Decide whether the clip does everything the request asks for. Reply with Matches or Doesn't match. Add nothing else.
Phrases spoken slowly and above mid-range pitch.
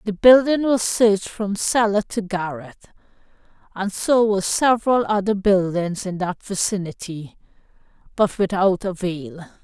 Matches